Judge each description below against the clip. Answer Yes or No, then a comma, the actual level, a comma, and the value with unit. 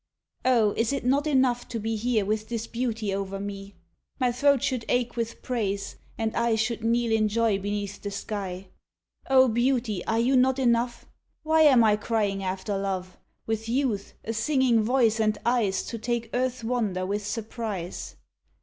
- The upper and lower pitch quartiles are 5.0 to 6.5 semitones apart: No, average, 3.1 semitones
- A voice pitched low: No, high, 225 Hz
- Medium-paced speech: Yes, average, 170 wpm